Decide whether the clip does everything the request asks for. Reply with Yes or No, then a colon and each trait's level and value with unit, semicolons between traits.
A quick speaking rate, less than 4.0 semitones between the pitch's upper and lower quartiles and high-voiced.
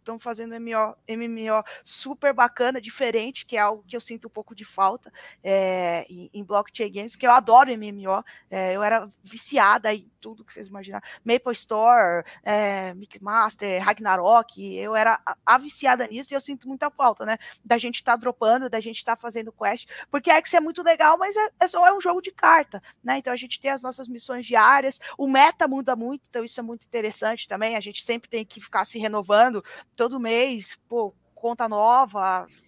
Yes: fast, 200 wpm; average, 3.4 semitones; high, 230 Hz